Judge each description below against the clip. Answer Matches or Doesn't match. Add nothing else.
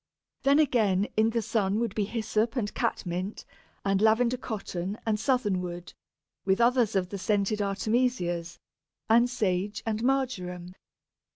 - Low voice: Doesn't match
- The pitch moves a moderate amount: Matches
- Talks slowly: Matches